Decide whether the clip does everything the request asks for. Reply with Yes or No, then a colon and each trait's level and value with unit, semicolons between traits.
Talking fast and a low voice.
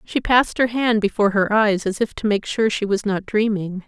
No: fast, 250 wpm; high, 210 Hz